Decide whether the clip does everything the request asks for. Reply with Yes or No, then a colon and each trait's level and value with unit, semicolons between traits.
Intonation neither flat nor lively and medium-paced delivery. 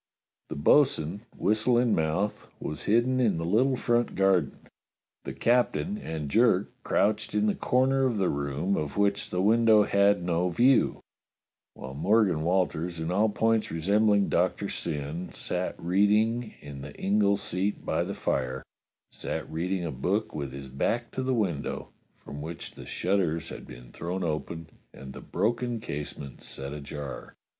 No: wide, 6.0 semitones; average, 165 wpm